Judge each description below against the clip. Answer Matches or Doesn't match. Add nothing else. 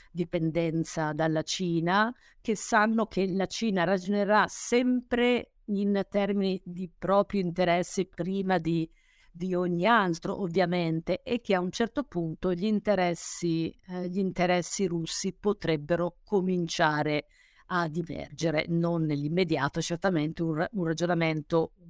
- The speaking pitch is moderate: Matches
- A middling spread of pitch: Matches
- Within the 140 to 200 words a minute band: Doesn't match